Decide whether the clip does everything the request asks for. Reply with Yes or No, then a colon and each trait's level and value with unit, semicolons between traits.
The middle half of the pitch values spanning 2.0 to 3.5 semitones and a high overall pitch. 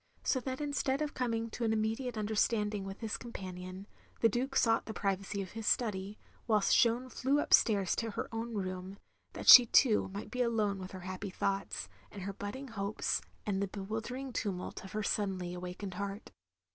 Yes: average, 3.2 semitones; high, 210 Hz